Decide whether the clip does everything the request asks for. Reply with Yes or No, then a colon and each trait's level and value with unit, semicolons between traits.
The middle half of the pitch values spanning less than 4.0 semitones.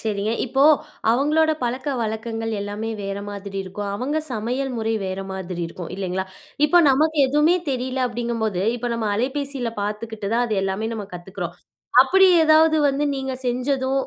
No: average, 4.7 semitones